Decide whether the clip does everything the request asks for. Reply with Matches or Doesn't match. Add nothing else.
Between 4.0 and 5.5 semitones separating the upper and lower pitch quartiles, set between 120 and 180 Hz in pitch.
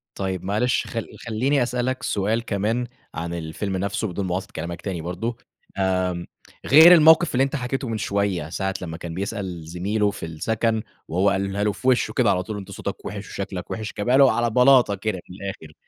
Doesn't match